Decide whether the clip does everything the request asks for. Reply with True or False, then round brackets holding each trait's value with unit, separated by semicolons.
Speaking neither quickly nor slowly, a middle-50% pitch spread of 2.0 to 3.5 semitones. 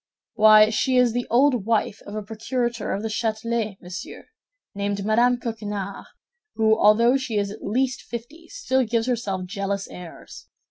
True (155 wpm; 2.9 semitones)